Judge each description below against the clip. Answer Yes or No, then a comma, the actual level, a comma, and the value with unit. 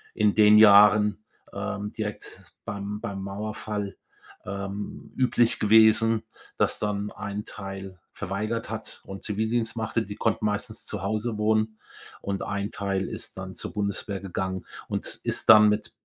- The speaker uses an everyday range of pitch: No, narrow, 1.6 semitones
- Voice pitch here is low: Yes, low, 105 Hz